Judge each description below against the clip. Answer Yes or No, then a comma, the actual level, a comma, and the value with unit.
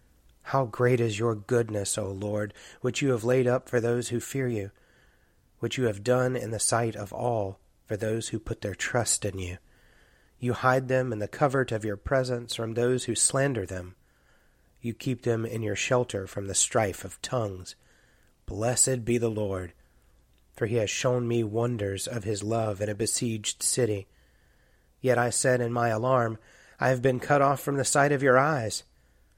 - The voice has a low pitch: Yes, low, 115 Hz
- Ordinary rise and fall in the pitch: Yes, average, 3.4 semitones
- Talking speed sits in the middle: Yes, average, 190 wpm